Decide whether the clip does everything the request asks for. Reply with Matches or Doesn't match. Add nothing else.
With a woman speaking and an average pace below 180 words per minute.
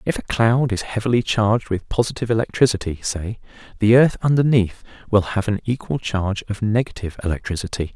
Doesn't match